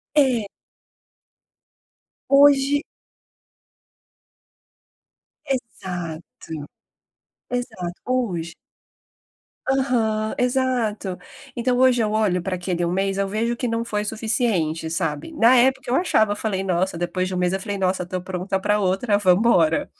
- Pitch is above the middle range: Yes, high, 210 Hz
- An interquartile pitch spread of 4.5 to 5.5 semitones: Yes, average, 5.1 semitones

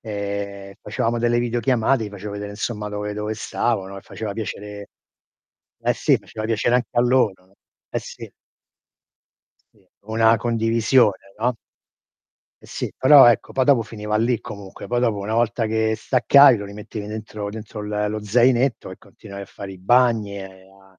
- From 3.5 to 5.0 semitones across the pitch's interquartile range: No, narrow, 2.6 semitones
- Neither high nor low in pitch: No, low, 110 Hz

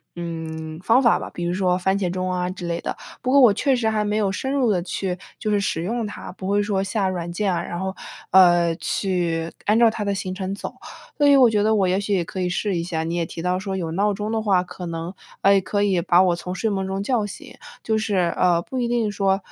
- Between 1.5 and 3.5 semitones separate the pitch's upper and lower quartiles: Yes, average, 3.0 semitones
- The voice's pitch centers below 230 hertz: Yes, high, 190 Hz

